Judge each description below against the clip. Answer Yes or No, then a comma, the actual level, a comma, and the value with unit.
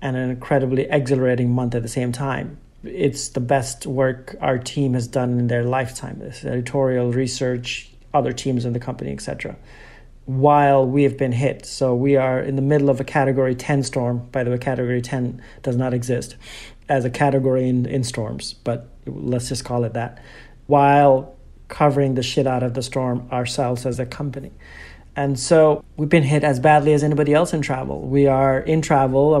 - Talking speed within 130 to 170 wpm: No, average, 190 wpm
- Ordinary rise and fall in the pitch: No, narrow, 2.0 semitones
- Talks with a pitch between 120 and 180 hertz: Yes, low, 130 Hz